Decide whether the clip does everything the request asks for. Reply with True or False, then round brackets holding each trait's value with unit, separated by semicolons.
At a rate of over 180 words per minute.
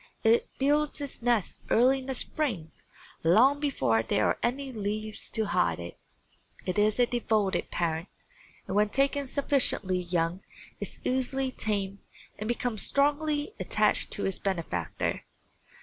False (140 wpm)